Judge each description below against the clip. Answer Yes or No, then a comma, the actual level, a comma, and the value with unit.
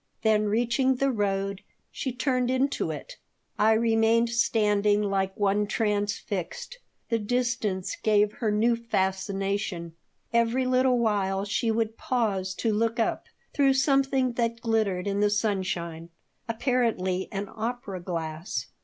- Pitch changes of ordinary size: Yes, average, 3.3 semitones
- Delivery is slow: Yes, slow, 125 wpm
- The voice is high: Yes, high, 215 Hz